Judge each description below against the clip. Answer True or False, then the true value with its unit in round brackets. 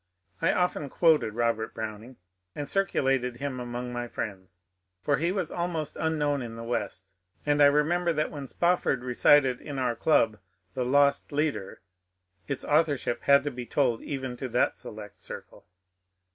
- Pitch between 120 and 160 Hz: True (135 Hz)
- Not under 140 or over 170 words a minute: True (160 wpm)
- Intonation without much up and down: False (3.8 semitones)